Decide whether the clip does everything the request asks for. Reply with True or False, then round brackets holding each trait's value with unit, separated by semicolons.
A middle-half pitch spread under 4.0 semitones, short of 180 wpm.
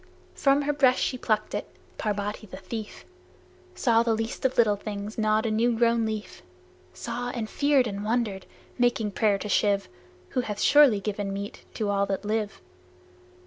True (2.7 semitones; 170 wpm)